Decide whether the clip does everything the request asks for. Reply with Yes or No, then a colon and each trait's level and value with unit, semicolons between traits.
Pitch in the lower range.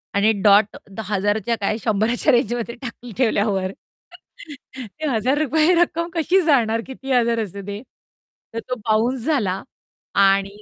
No: high, 230 Hz